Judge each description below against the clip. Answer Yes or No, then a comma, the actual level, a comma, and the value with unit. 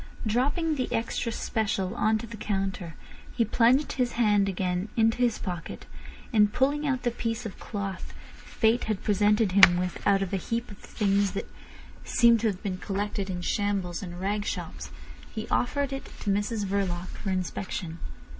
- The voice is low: No, high, 205 Hz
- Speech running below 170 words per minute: No, average, 175 wpm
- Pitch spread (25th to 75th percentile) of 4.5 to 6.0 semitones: No, average, 3.1 semitones